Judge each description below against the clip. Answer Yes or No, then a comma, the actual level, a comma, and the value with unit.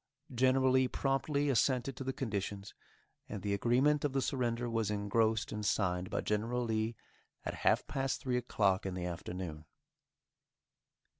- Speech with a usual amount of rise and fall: Yes, average, 4.4 semitones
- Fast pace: No, average, 150 wpm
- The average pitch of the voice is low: Yes, low, 115 Hz